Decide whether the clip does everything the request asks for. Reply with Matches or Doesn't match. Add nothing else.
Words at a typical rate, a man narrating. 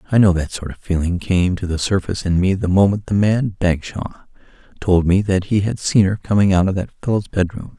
Doesn't match